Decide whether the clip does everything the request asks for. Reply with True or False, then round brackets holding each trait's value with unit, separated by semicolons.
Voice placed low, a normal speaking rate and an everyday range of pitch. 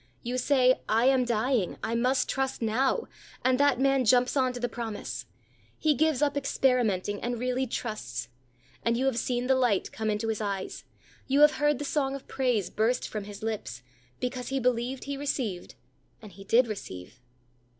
False (245 Hz; 180 wpm; 3.5 semitones)